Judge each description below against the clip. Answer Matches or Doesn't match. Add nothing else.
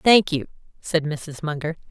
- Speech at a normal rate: Matches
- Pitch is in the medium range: Matches